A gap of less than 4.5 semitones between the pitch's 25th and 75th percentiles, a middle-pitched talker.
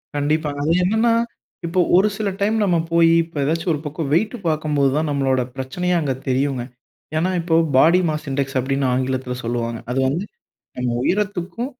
No: average, 4.8 semitones; medium, 150 Hz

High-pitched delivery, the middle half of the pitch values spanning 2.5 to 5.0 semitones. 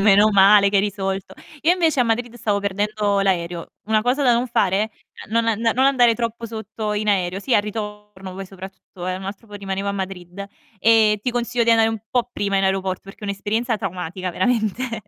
Yes: high, 210 Hz; average, 2.8 semitones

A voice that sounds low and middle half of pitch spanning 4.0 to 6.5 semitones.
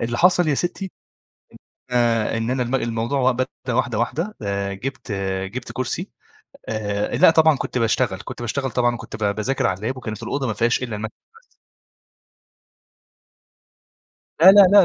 No: low, 120 Hz; average, 3.3 semitones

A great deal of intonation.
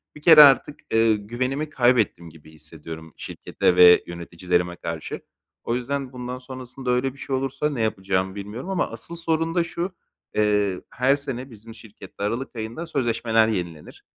Yes: wide, 6.0 semitones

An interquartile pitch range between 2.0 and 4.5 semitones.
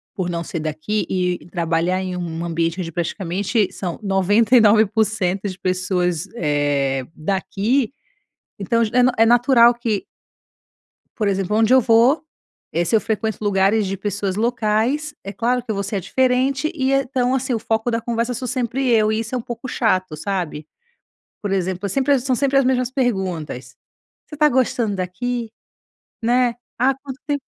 No: average, 5.0 semitones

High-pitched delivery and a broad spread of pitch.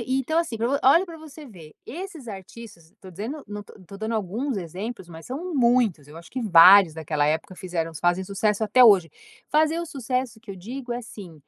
Yes: high, 220 Hz; wide, 6.6 semitones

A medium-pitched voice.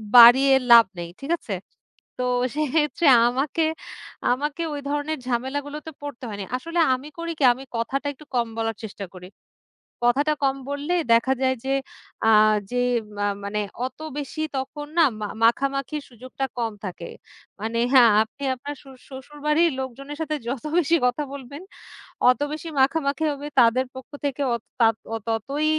No: very high, 270 Hz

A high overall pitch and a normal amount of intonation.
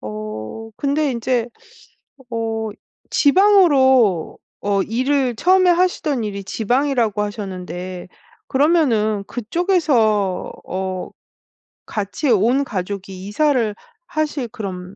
No: high, 225 Hz; wide, 6.0 semitones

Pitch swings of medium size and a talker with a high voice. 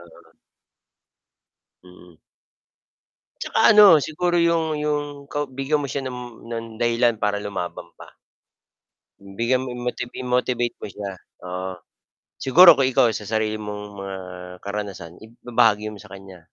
No: average, 4.9 semitones; low, 115 Hz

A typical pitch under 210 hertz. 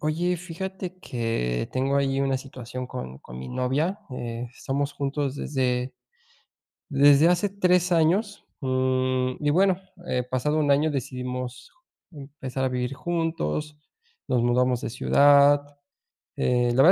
Yes: low, 135 Hz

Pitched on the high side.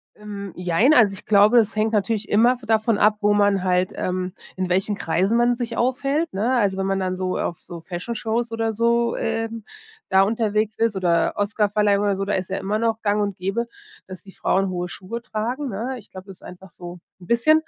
Yes: high, 210 Hz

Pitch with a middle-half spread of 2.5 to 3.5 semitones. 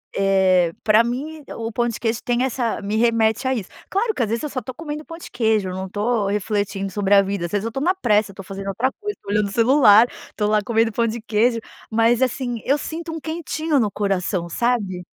No: average, 4.1 semitones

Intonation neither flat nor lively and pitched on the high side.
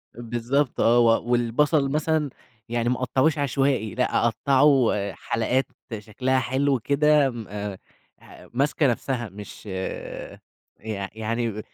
No: average, 3.6 semitones; low, 120 Hz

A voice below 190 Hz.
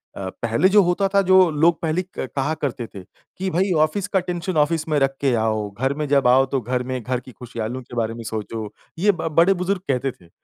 Yes: medium, 140 Hz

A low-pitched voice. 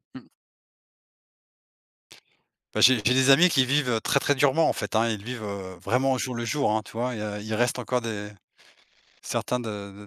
Yes: low, 120 Hz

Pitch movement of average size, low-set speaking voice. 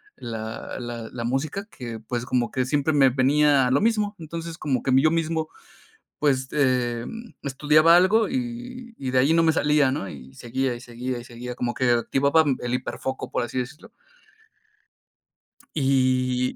Yes: average, 4.2 semitones; low, 130 Hz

